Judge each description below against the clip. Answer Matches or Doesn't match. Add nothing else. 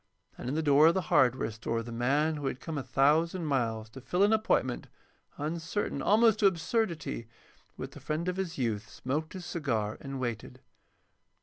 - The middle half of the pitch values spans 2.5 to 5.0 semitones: Doesn't match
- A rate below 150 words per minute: Doesn't match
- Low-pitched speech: Doesn't match